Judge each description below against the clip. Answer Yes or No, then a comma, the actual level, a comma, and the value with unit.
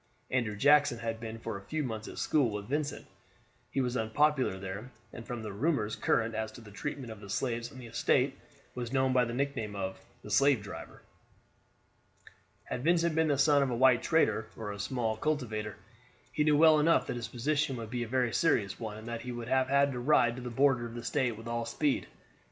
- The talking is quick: Yes, fast, 220 wpm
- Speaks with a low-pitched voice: Yes, low, 120 Hz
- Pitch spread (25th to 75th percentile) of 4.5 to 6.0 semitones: No, average, 3.9 semitones